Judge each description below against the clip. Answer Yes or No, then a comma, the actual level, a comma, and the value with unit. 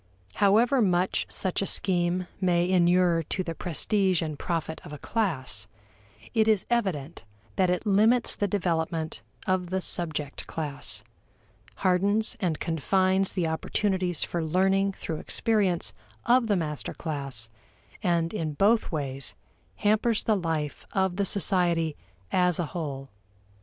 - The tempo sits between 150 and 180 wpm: No, slow, 135 wpm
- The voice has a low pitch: No, medium, 180 Hz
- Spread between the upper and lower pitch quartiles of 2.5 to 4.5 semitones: Yes, average, 3.5 semitones